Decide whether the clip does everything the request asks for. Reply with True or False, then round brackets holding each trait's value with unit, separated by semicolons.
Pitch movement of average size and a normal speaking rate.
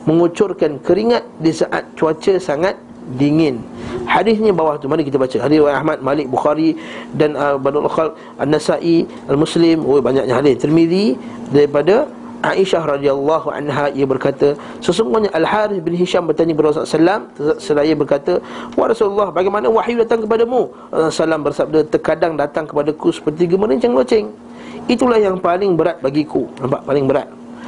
True (4.9 semitones; 145 wpm)